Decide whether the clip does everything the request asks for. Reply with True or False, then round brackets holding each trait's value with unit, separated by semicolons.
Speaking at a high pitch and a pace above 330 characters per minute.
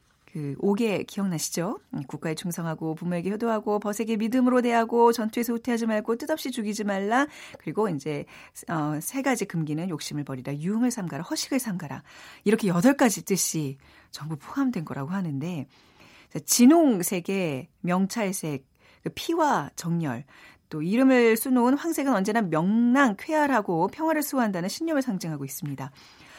True (200 Hz; 340 characters per minute)